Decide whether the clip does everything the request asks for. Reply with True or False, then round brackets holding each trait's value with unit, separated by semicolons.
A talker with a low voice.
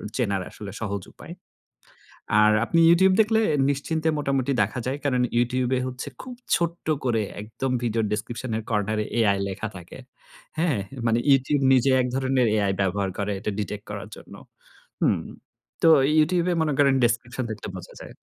True (125 Hz)